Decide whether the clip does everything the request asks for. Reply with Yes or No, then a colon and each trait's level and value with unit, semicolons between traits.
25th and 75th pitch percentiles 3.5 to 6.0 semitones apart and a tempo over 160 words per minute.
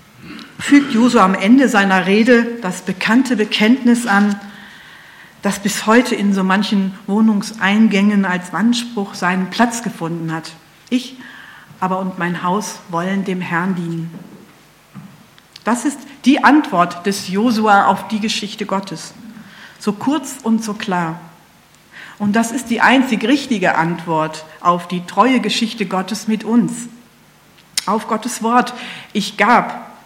No: average, 3.9 semitones; average, 130 wpm